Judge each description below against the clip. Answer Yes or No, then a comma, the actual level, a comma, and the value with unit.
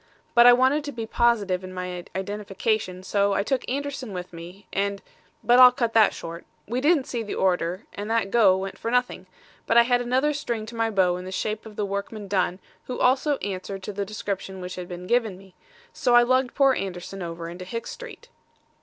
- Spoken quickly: Yes, fast, 215 wpm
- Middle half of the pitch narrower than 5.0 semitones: Yes, average, 4.6 semitones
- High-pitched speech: Yes, high, 210 Hz